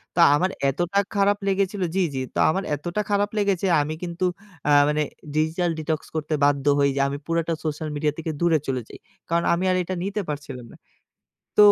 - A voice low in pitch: No, medium, 165 Hz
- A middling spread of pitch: Yes, average, 4.2 semitones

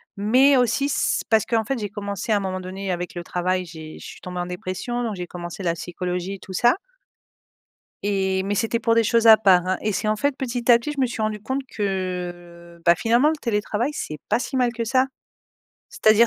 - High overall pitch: Yes, high, 205 Hz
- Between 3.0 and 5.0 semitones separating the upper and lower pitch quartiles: Yes, average, 4.5 semitones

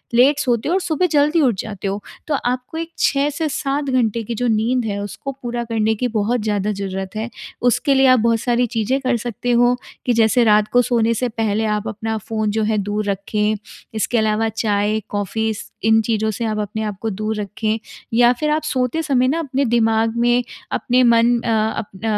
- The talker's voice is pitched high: Yes, high, 225 Hz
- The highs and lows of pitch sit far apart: No, average, 2.7 semitones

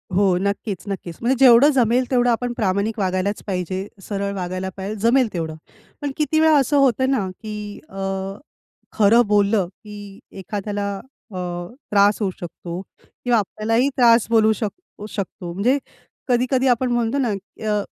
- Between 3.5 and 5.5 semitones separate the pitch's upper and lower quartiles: Yes, average, 3.9 semitones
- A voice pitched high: Yes, high, 210 Hz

